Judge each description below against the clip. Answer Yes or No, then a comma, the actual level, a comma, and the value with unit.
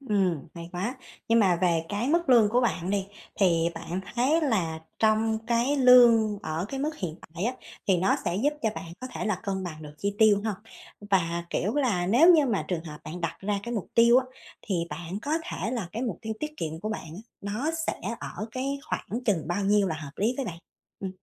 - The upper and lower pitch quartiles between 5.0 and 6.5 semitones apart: Yes, wide, 5.5 semitones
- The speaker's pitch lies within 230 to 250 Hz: No, high, 205 Hz